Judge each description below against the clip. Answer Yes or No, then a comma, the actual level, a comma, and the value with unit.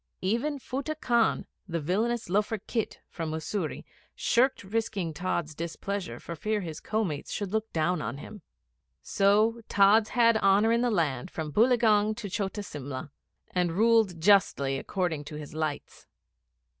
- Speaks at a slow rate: No, average, 150 wpm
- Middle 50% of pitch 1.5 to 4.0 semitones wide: No, wide, 5.5 semitones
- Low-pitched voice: No, high, 200 Hz